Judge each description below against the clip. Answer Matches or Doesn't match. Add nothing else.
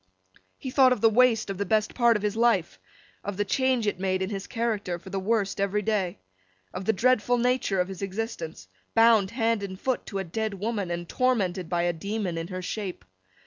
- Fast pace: Matches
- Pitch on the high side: Matches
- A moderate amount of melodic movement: Matches